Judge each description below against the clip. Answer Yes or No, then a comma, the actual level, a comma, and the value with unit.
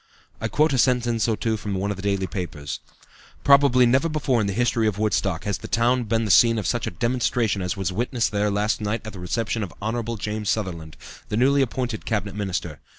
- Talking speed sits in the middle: No, fast, 220 wpm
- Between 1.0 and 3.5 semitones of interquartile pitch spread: Yes, average, 3.2 semitones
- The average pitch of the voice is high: No, low, 110 Hz